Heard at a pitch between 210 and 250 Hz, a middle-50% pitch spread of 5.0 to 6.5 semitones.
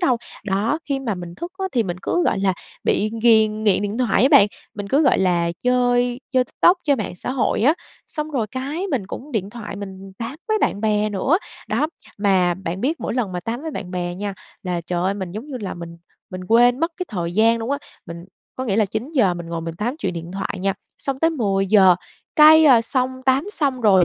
Yes: high, 220 Hz; wide, 5.6 semitones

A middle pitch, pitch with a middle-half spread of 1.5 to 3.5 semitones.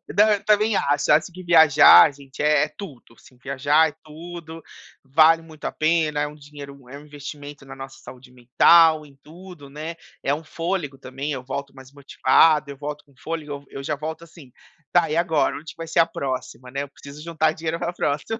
Yes: medium, 150 Hz; average, 2.7 semitones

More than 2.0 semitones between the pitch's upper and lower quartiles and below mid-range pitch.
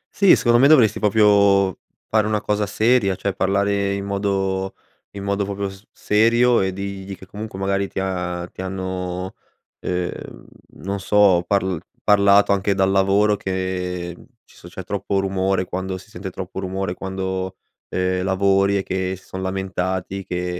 No: narrow, 1.2 semitones; very low, 95 Hz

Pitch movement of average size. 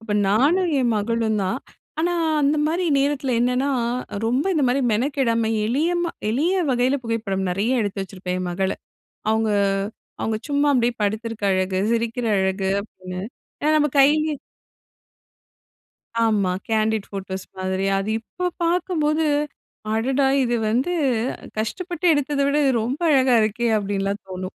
No: wide, 5.7 semitones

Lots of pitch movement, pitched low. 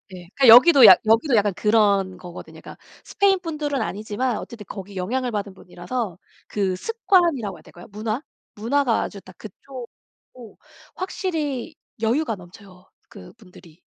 No: wide, 5.7 semitones; high, 220 Hz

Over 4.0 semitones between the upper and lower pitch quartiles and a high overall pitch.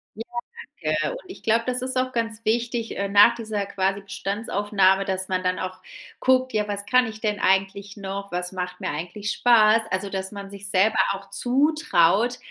No: average, 3.0 semitones; high, 205 Hz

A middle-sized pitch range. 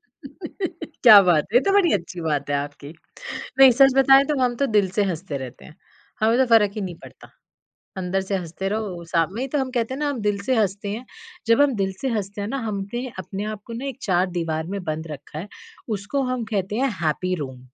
No: wide, 6.6 semitones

